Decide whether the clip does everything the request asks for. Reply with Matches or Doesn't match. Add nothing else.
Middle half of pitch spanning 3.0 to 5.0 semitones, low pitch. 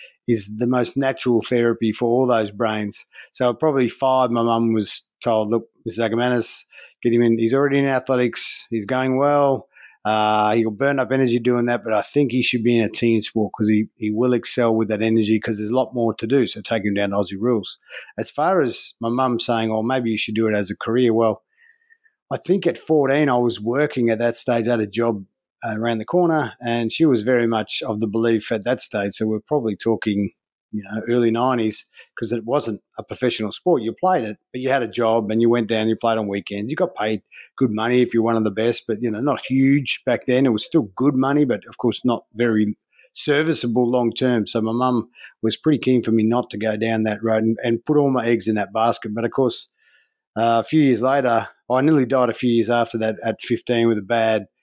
Doesn't match